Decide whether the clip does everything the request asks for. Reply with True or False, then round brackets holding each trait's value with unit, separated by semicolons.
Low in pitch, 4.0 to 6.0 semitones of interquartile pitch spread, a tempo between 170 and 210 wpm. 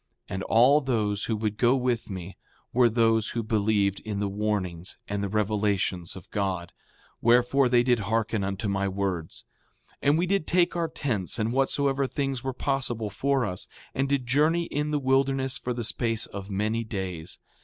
True (115 Hz; 4.9 semitones; 180 wpm)